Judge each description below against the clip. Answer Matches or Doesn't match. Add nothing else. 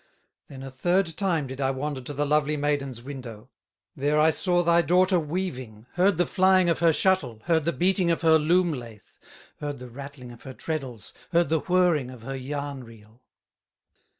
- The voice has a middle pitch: Matches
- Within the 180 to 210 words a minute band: Matches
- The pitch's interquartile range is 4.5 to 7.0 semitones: Matches